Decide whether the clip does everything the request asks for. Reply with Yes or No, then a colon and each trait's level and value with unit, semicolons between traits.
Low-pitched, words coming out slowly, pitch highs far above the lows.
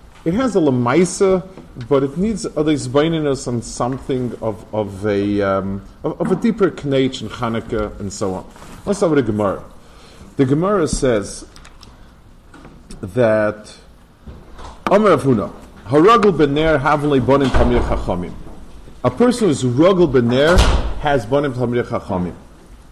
Yes: low, 130 Hz; slow, 120 wpm; wide, 6.1 semitones